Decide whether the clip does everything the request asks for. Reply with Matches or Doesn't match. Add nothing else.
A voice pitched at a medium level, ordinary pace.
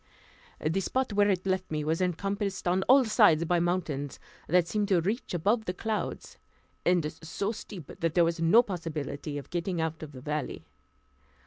Matches